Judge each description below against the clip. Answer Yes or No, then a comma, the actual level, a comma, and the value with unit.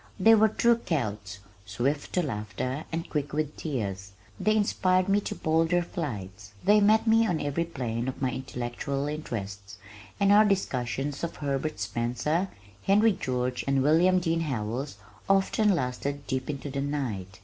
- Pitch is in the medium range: Yes, medium, 145 Hz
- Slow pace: No, average, 155 wpm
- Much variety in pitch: Yes, wide, 6.6 semitones